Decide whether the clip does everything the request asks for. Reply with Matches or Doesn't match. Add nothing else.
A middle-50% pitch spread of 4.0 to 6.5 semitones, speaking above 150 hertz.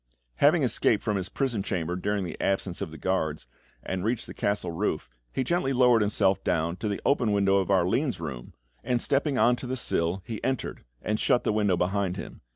Doesn't match